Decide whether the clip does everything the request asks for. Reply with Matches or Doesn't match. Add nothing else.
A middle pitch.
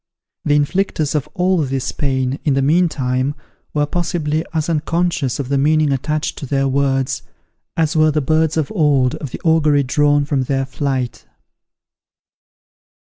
Matches